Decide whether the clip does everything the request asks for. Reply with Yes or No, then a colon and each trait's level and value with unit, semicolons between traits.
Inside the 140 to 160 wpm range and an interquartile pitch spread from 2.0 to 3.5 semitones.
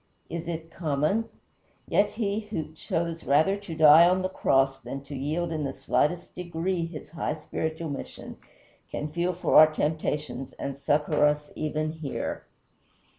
Yes: average, 155 wpm; narrow, 2.6 semitones